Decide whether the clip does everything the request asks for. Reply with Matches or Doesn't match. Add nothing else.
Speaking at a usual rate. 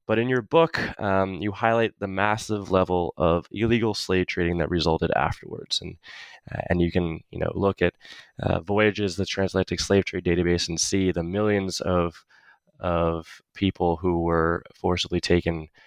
Matches